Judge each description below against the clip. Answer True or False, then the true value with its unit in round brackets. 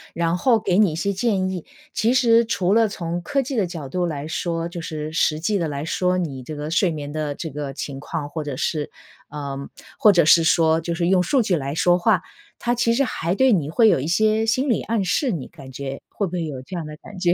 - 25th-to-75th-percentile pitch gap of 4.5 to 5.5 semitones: True (4.8 semitones)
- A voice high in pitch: False (170 Hz)